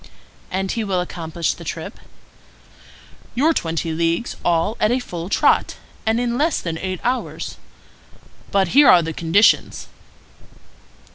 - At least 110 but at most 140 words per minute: Yes, slow, 135 wpm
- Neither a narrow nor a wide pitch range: No, wide, 6.0 semitones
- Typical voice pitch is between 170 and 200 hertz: Yes, medium, 185 Hz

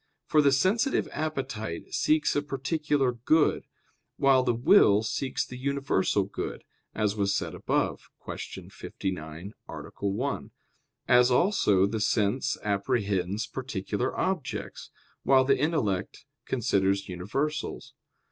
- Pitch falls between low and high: No, low, 125 Hz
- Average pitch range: No, wide, 5.8 semitones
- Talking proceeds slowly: Yes, slow, 115 wpm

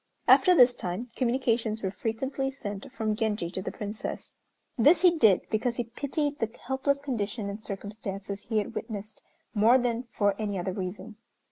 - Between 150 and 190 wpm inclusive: Yes, average, 165 wpm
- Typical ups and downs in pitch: Yes, average, 3.9 semitones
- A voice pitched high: Yes, high, 220 Hz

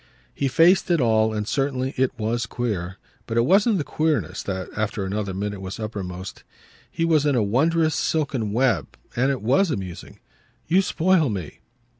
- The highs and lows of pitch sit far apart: Yes, wide, 6.8 semitones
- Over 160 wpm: Yes, average, 170 wpm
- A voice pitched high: No, low, 120 Hz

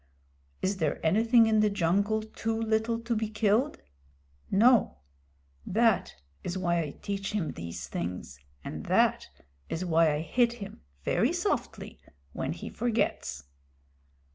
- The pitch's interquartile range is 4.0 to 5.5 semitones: Yes, average, 4.8 semitones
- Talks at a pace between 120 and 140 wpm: Yes, slow, 135 wpm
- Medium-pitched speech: No, high, 210 Hz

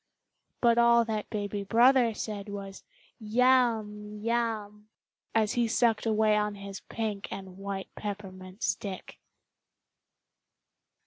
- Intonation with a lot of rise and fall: No, narrow, 2.4 semitones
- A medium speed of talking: No, slow, 110 wpm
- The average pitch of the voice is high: Yes, high, 210 Hz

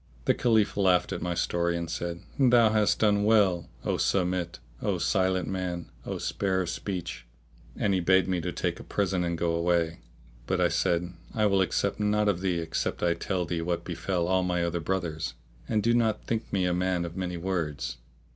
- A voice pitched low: Yes, very low, 90 Hz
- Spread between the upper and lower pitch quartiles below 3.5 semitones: Yes, narrow, 2.5 semitones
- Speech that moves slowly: No, average, 195 wpm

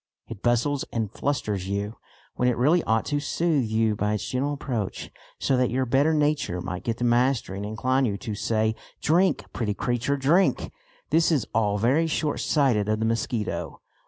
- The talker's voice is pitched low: Yes, low, 120 Hz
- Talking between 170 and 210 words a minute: Yes, average, 180 wpm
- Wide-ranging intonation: No, average, 4.9 semitones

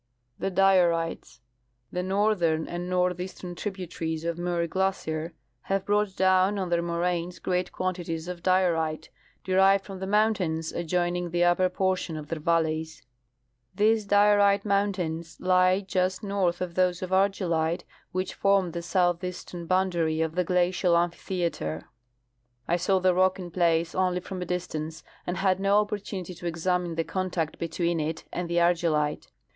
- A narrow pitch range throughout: Yes, narrow, 2.0 semitones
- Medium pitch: Yes, medium, 180 Hz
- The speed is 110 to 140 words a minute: No, average, 155 wpm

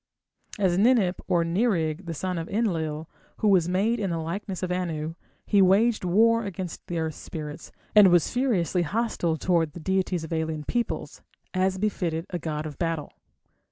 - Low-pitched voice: No, medium, 180 Hz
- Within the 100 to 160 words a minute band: No, average, 170 wpm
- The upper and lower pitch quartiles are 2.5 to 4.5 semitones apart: Yes, average, 3.5 semitones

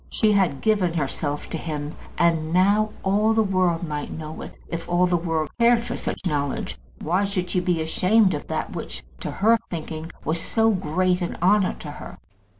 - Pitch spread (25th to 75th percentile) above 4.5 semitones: No, average, 4.0 semitones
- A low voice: No, medium, 180 Hz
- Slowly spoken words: No, average, 190 wpm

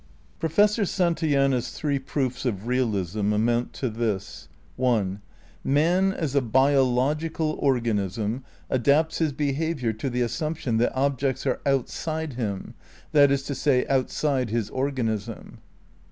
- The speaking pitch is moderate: No, low, 130 Hz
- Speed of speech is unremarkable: No, slow, 125 wpm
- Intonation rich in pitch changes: No, average, 4.0 semitones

